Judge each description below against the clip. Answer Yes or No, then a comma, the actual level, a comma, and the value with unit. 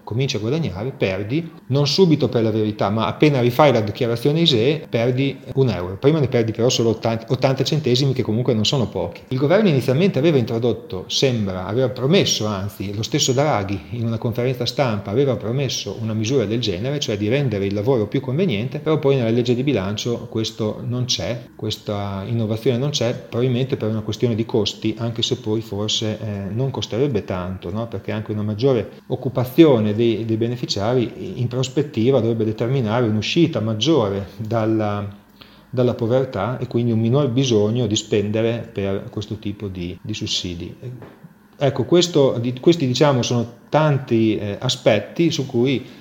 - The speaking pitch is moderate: No, low, 120 Hz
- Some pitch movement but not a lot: Yes, average, 4.0 semitones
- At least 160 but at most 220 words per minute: Yes, average, 165 wpm